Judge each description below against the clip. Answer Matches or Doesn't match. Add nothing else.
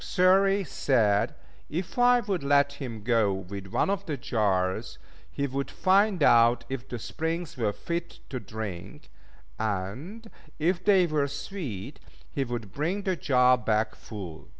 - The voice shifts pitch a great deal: Matches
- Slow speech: Doesn't match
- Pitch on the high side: Doesn't match